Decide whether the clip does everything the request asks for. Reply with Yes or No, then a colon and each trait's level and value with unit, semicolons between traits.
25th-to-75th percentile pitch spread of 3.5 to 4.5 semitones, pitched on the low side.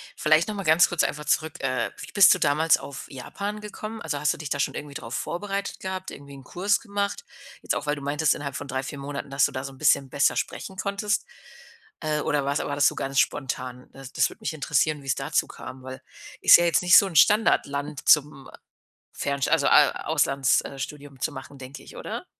No: average, 4.2 semitones; medium, 145 Hz